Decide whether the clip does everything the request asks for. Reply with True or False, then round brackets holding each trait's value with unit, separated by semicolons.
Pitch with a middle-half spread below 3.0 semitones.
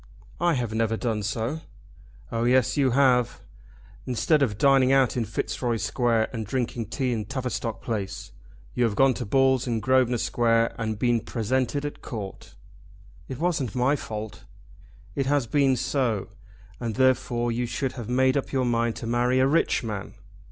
True (2.5 semitones)